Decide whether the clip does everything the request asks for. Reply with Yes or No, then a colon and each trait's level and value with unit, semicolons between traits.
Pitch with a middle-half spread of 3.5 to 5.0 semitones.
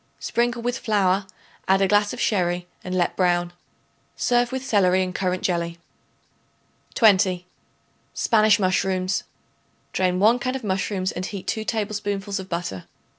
No: average, 2.9 semitones